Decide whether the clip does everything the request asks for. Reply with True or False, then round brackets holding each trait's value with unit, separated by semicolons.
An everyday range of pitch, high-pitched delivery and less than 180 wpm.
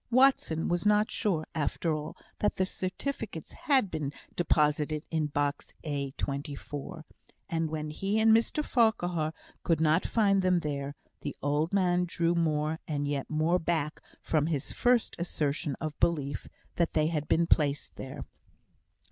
False (3.5 semitones; 160 Hz; 150 wpm)